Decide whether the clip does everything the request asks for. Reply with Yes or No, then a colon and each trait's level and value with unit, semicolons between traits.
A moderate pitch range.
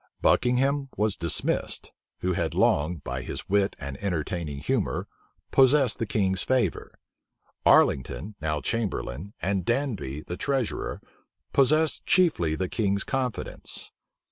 No: wide, 8.2 semitones